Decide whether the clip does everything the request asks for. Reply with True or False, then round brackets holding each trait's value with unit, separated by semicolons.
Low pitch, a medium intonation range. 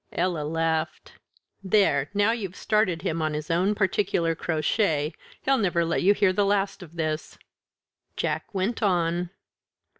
False (175 Hz; 3.7 semitones)